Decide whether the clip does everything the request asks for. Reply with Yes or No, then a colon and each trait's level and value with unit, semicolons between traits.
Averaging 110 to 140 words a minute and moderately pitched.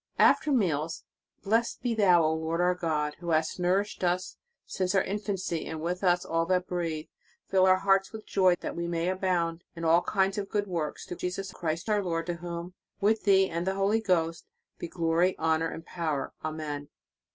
No: average, 195 wpm; medium, 175 Hz